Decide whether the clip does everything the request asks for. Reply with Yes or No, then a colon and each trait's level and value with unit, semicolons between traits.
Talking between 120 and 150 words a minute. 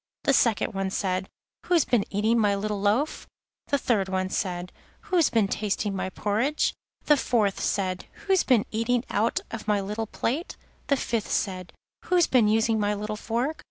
No: average, 160 wpm